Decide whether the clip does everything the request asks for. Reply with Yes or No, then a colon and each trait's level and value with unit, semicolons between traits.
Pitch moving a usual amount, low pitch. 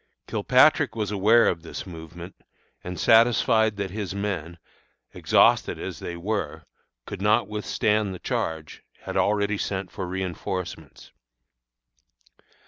Yes: average, 3.3 semitones; very low, 95 Hz